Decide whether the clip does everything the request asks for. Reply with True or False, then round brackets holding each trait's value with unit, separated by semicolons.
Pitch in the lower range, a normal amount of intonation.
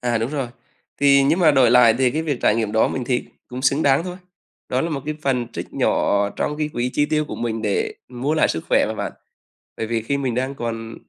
True (130 Hz; 3.7 semitones)